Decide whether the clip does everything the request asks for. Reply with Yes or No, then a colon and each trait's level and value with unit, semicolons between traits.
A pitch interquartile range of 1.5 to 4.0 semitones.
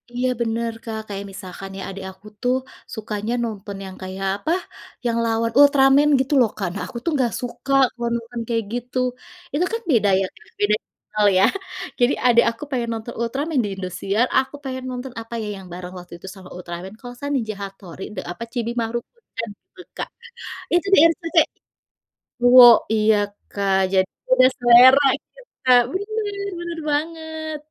No: average, 4.7 semitones